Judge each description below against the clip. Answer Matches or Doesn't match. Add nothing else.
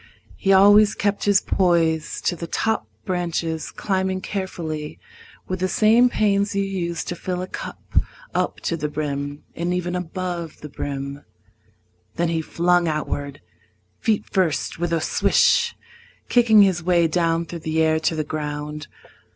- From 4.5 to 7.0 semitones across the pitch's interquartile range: Doesn't match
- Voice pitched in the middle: Matches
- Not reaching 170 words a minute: Matches